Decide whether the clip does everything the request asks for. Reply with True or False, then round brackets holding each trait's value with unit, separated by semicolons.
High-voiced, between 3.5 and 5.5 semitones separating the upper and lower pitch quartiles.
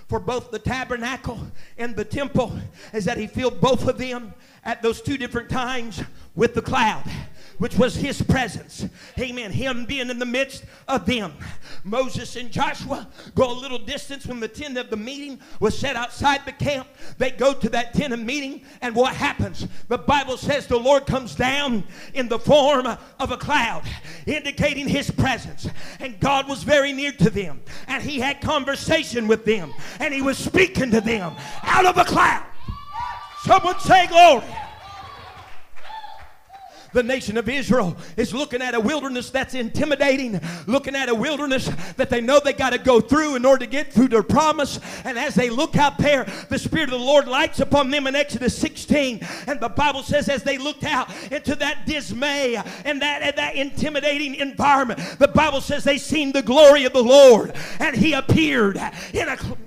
False (265 Hz; 3.1 semitones)